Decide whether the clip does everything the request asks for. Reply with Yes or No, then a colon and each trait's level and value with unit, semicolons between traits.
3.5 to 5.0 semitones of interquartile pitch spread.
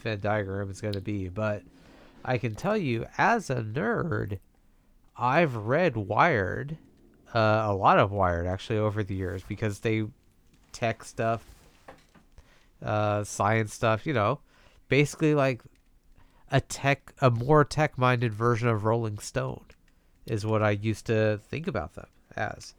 Yes: average, 3.8 semitones